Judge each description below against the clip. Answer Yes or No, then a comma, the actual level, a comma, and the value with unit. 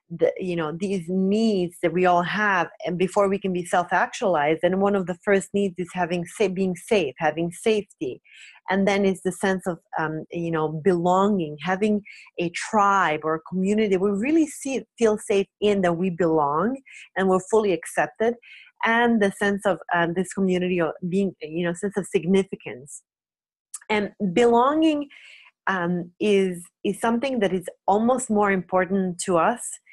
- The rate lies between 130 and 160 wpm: No, average, 170 wpm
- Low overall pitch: No, high, 190 Hz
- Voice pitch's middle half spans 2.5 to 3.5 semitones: Yes, average, 2.9 semitones